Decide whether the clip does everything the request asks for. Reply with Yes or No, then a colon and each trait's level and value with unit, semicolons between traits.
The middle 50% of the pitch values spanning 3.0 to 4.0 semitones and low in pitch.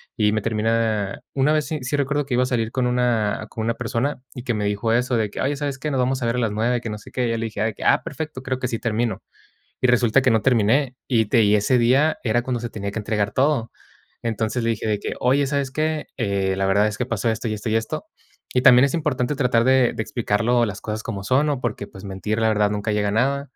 Yes: average, 3.3 semitones; low, 115 Hz